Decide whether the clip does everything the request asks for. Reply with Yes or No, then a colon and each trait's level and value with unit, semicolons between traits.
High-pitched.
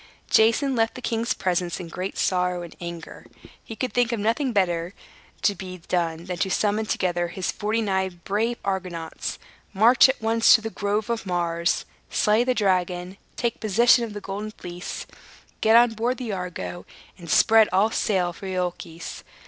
Yes: high, 195 Hz